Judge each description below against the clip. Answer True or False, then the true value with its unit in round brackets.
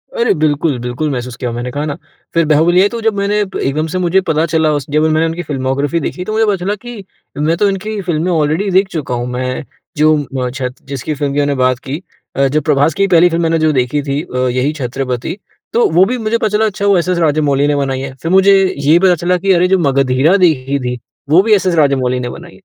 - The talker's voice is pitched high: False (155 Hz)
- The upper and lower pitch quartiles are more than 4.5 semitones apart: True (5.0 semitones)